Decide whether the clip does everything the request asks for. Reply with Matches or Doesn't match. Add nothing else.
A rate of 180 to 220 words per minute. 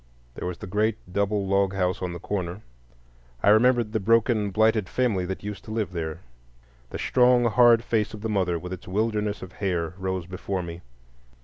Matches